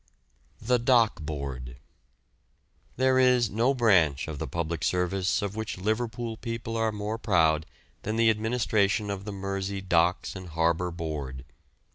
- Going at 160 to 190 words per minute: No, average, 140 wpm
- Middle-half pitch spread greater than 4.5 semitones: Yes, average, 5.2 semitones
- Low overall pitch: Yes, low, 100 Hz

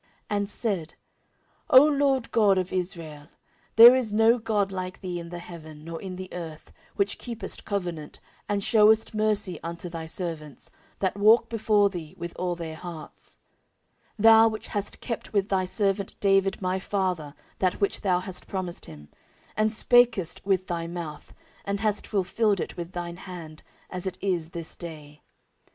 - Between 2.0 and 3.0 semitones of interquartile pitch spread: No, average, 3.5 semitones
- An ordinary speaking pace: Yes, average, 170 wpm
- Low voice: No, medium, 185 Hz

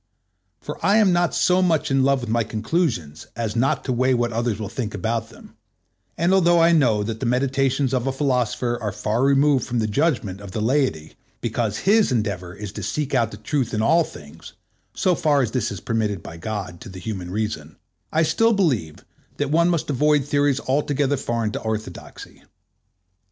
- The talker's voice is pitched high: No, low, 120 Hz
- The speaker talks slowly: No, average, 195 wpm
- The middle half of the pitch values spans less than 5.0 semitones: No, average, 5.3 semitones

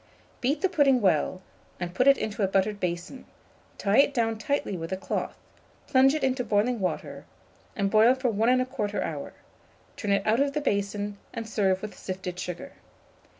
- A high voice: Yes, high, 215 Hz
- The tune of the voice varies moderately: Yes, average, 4.8 semitones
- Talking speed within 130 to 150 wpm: No, average, 180 wpm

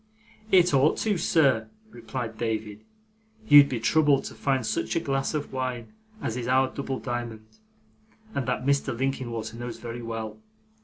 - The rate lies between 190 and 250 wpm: No, average, 155 wpm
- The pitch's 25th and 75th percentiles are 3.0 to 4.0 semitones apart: Yes, average, 3.5 semitones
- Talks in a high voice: No, low, 125 Hz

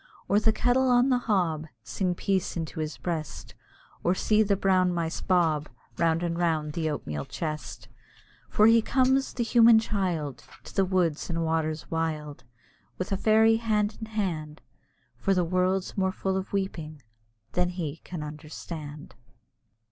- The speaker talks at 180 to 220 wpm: No, average, 155 wpm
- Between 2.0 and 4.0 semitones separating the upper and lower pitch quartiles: No, average, 4.6 semitones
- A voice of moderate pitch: Yes, medium, 180 Hz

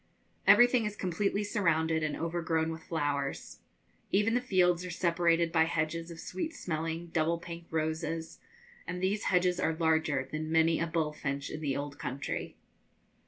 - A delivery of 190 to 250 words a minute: No, average, 160 wpm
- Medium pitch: Yes, medium, 165 Hz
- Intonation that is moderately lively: No, narrow, 2.1 semitones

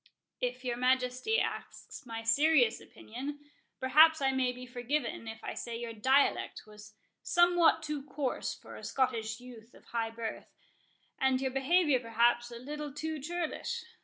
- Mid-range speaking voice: No, very high, 255 Hz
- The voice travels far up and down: No, average, 3.8 semitones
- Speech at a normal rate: Yes, average, 155 wpm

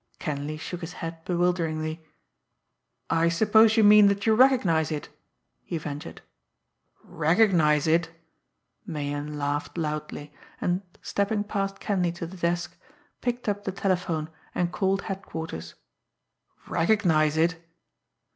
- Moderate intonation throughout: Yes, average, 3.9 semitones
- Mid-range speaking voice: Yes, medium, 170 Hz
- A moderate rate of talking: No, slow, 120 wpm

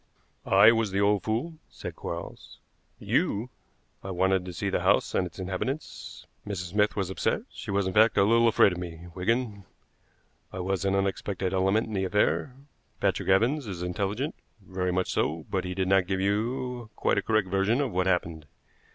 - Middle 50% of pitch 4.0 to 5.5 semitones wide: No, average, 2.8 semitones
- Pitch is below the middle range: Yes, very low, 95 Hz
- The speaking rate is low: No, average, 185 wpm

